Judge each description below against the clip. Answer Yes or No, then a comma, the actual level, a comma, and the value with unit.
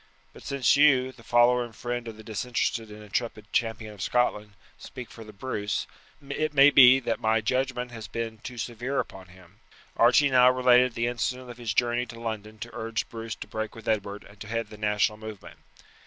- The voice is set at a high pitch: No, low, 115 Hz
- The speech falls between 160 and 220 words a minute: Yes, average, 200 wpm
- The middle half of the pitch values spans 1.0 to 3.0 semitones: Yes, narrow, 2.5 semitones